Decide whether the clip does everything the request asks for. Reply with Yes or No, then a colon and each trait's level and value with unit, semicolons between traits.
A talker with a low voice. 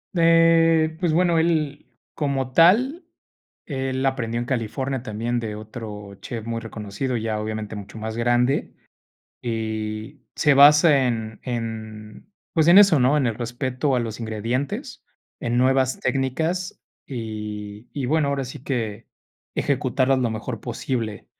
Yes: low, 125 Hz